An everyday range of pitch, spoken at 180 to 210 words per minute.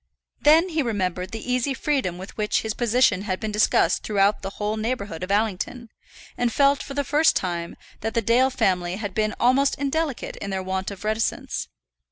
Yes: average, 4.9 semitones; average, 190 wpm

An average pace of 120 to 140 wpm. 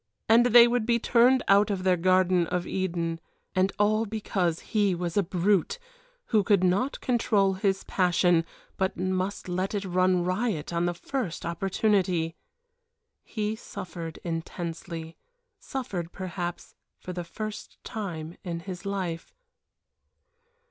Yes: slow, 135 wpm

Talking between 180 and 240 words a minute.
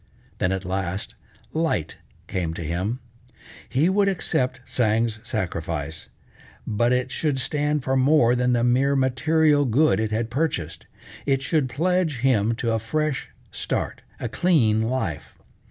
No: average, 140 wpm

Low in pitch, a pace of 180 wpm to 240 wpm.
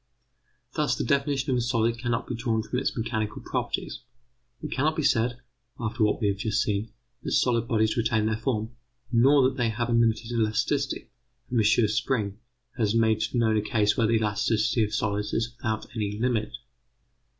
Yes: low, 115 Hz; average, 185 wpm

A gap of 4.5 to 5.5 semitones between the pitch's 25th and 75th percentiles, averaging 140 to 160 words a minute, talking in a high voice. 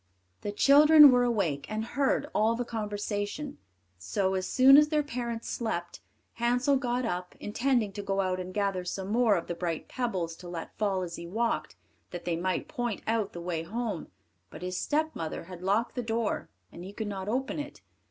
No: average, 4.9 semitones; average, 190 wpm; high, 210 Hz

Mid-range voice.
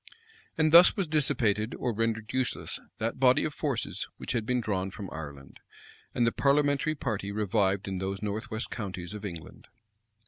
No: low, 110 Hz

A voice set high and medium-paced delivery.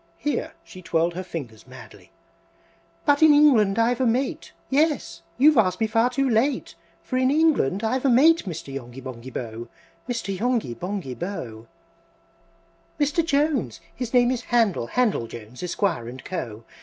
Yes: high, 220 Hz; average, 160 wpm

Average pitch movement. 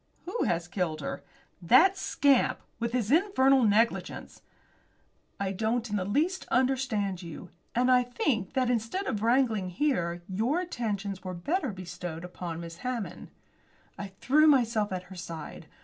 No: wide, 6.1 semitones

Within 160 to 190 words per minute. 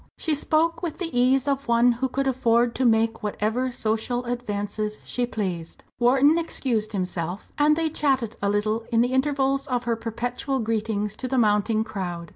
Yes: average, 175 wpm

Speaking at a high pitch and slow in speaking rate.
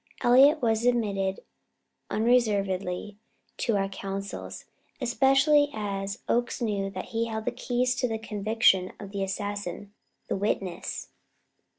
Yes: high, 210 Hz; slow, 120 wpm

